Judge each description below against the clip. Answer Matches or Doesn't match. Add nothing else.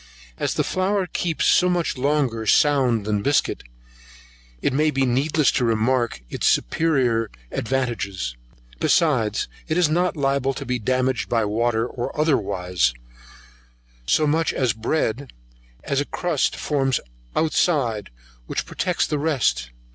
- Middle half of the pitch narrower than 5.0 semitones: Doesn't match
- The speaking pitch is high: Doesn't match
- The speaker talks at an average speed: Doesn't match